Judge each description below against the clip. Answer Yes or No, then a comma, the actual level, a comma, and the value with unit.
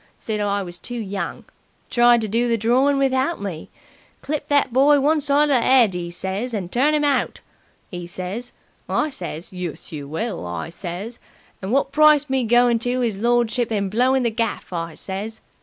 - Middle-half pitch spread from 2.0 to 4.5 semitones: No, wide, 5.5 semitones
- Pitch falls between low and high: No, high, 235 Hz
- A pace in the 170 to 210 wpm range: Yes, average, 190 wpm